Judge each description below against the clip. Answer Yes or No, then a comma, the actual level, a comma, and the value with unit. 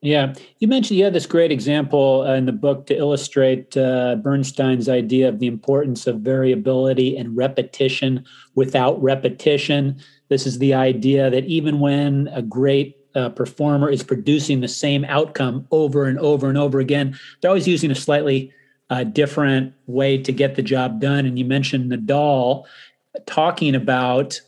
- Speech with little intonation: Yes, narrow, 1.6 semitones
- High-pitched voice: No, low, 135 Hz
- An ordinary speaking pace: Yes, average, 165 wpm